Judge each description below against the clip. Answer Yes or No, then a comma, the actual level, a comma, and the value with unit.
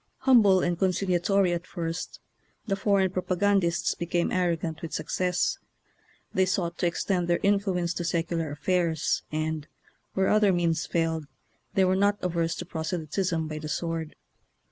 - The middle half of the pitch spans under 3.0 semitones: Yes, narrow, 2.4 semitones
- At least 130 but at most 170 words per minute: Yes, average, 155 wpm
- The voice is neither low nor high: Yes, medium, 175 Hz